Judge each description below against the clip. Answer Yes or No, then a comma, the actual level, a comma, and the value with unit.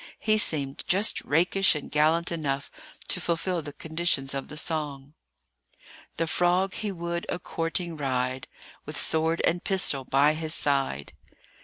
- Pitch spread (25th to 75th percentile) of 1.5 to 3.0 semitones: No, average, 3.5 semitones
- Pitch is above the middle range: No, medium, 160 Hz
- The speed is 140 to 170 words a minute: Yes, average, 145 wpm